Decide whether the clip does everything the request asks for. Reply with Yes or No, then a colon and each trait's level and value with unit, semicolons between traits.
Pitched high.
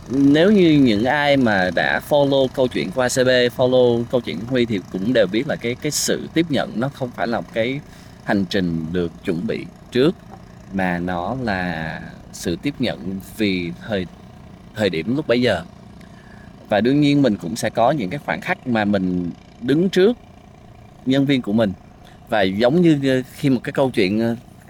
No: low, 120 Hz